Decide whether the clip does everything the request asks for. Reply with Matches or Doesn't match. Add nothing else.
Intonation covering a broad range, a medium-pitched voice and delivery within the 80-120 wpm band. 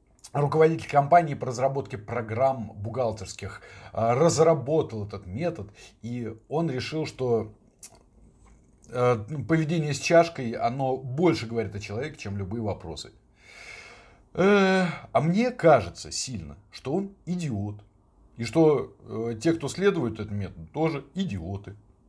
Doesn't match